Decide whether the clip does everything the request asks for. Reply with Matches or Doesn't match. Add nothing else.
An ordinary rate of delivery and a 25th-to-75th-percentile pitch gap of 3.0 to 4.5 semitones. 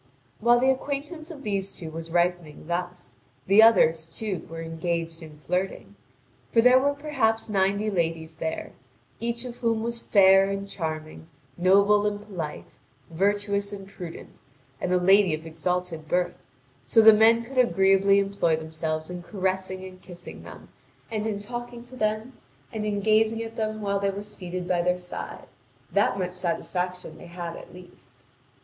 Matches